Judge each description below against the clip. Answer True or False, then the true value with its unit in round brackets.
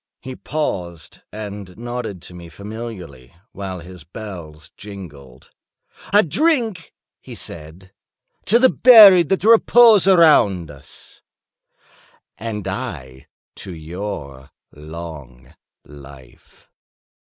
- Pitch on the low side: True (95 Hz)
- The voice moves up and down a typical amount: False (8.9 semitones)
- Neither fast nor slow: False (95 wpm)